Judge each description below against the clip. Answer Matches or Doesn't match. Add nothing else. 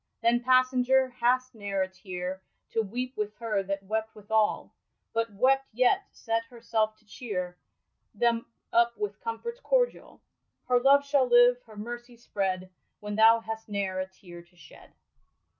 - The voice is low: Doesn't match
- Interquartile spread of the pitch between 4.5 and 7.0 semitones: Doesn't match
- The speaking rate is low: Doesn't match